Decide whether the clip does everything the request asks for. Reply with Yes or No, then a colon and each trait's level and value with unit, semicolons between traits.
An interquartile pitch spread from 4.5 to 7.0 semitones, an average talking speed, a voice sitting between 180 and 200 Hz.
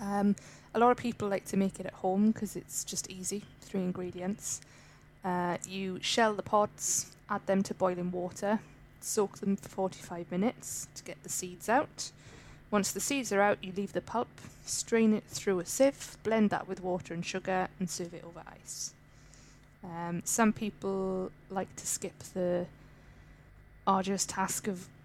No: narrow, 2.5 semitones; average, 175 wpm; high, 190 Hz